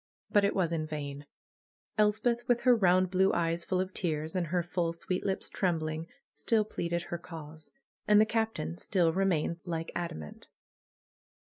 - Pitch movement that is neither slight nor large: Yes, average, 3.2 semitones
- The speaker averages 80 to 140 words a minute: No, average, 160 wpm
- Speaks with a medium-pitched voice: Yes, medium, 175 Hz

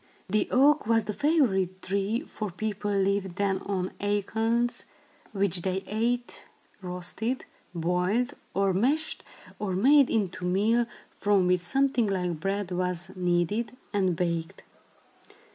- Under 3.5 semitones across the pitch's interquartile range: No, average, 3.8 semitones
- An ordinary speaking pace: No, slow, 125 wpm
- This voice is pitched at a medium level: No, high, 200 Hz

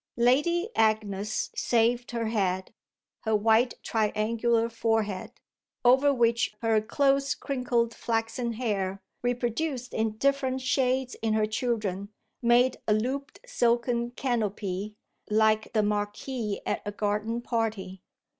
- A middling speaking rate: No, slow, 115 wpm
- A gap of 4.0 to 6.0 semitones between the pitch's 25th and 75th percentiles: No, narrow, 2.6 semitones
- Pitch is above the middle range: Yes, high, 230 Hz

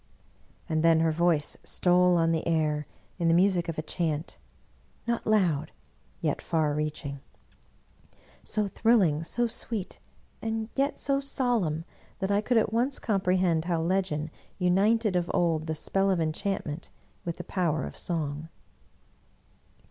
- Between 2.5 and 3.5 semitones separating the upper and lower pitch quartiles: No, average, 4.1 semitones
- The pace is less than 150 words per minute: Yes, average, 140 wpm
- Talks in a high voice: No, medium, 175 Hz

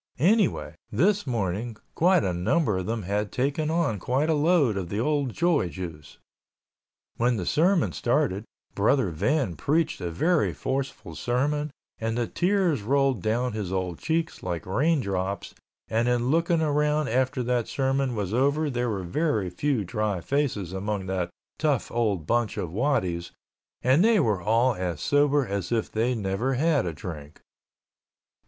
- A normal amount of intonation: No, wide, 7.1 semitones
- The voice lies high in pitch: No, low, 120 Hz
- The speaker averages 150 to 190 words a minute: Yes, average, 160 wpm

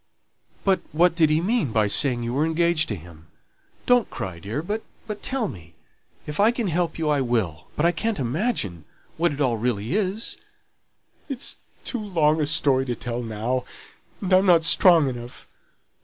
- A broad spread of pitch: Yes, wide, 7.2 semitones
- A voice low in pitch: No, medium, 150 Hz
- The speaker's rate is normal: Yes, average, 175 wpm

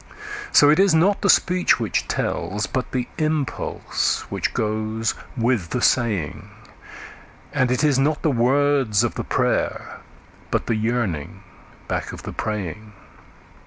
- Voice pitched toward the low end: Yes, low, 125 Hz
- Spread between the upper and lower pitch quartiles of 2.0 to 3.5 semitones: No, average, 5.1 semitones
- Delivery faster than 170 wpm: No, average, 140 wpm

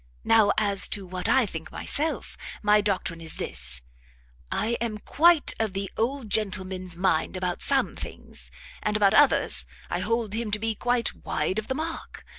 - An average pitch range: Yes, average, 3.8 semitones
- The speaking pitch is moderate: No, high, 210 Hz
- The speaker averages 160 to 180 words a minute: Yes, average, 170 wpm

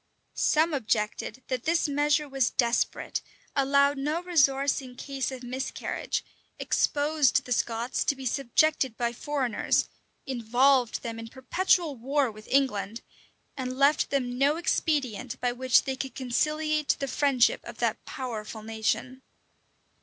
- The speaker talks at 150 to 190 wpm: No, slow, 135 wpm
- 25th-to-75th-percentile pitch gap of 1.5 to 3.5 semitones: Yes, average, 2.9 semitones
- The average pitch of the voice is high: Yes, very high, 265 Hz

